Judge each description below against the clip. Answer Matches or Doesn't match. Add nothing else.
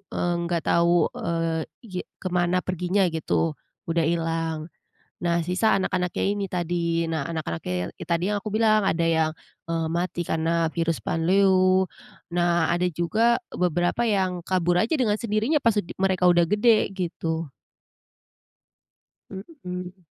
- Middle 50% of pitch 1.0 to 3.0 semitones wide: Matches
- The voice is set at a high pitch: Doesn't match